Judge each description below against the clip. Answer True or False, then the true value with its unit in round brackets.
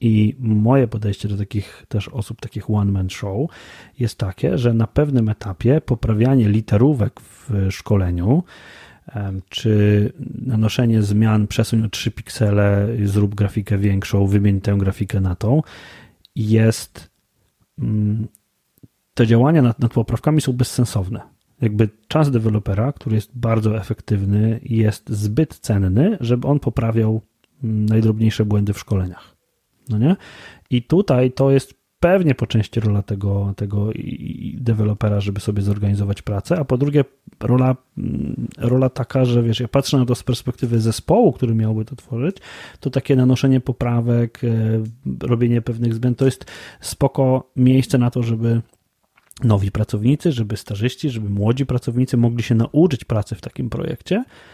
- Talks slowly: False (135 wpm)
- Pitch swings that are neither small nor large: True (3.4 semitones)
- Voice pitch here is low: True (115 Hz)